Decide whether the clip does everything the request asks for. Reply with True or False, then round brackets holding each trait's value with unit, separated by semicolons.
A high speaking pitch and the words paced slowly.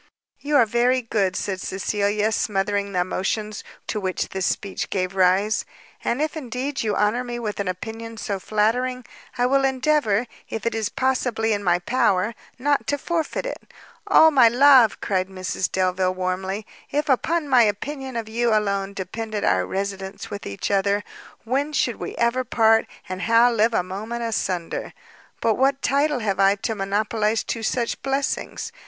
False (220 Hz; 170 wpm)